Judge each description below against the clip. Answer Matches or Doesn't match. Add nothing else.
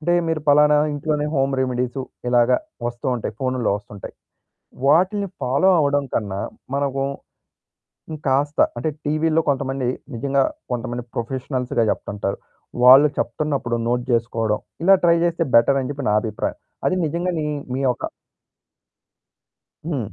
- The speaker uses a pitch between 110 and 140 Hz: Matches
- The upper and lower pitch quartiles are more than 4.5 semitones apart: Doesn't match